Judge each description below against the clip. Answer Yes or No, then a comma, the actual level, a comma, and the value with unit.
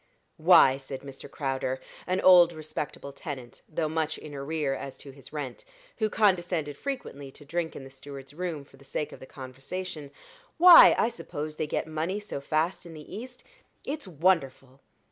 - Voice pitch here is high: No, medium, 155 Hz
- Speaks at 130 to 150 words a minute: No, average, 175 wpm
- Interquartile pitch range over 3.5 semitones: Yes, average, 4.3 semitones